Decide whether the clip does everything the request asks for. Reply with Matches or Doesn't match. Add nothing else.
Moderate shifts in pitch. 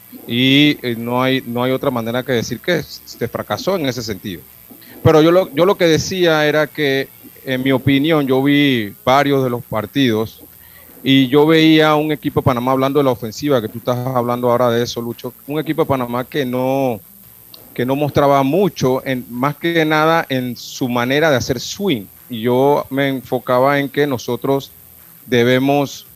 Matches